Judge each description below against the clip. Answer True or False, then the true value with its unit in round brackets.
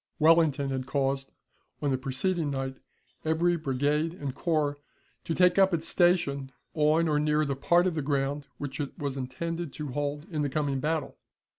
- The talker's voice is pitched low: False (150 Hz)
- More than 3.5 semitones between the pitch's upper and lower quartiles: False (3.0 semitones)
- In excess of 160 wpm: True (175 wpm)